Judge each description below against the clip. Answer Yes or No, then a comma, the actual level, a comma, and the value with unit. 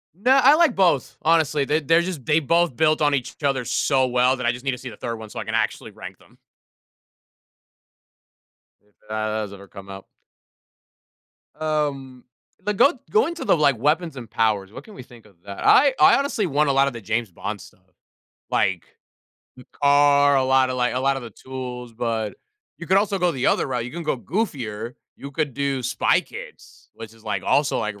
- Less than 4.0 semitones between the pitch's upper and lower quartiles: No, average, 4.9 semitones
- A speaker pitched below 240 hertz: Yes, low, 135 Hz